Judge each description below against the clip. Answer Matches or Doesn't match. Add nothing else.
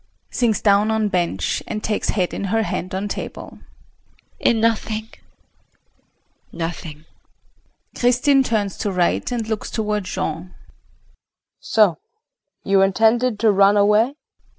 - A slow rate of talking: Matches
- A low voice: Doesn't match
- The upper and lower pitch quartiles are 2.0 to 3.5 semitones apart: Matches